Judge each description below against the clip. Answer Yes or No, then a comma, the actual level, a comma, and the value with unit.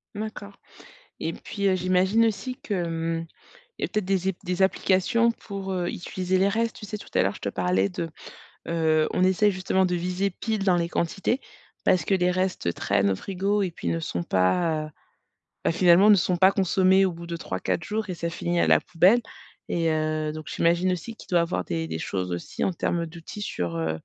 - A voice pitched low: No, medium, 180 Hz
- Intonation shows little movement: No, average, 3.1 semitones